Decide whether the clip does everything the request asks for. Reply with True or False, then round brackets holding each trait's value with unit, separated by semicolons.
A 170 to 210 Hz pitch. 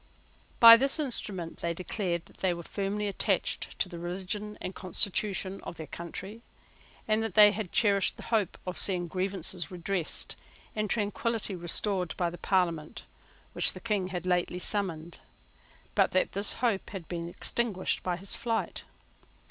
True (190 Hz)